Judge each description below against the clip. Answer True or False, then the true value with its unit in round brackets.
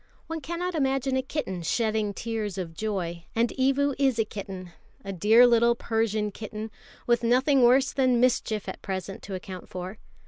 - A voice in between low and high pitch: False (225 Hz)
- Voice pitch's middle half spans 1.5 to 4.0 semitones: False (4.8 semitones)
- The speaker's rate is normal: True (170 wpm)